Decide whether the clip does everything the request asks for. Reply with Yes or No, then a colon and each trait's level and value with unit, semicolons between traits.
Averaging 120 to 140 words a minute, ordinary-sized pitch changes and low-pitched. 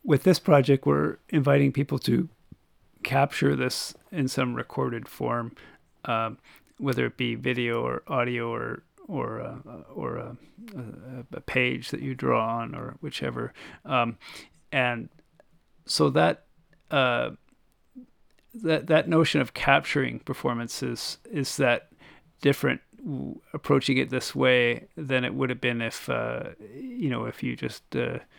Yes: slow, 135 wpm; average, 3.9 semitones; low, 130 Hz